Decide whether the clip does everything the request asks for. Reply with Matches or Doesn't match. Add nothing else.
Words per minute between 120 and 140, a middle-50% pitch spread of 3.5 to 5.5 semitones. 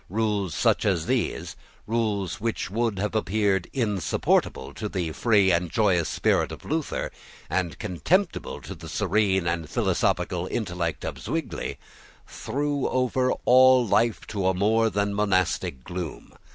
Matches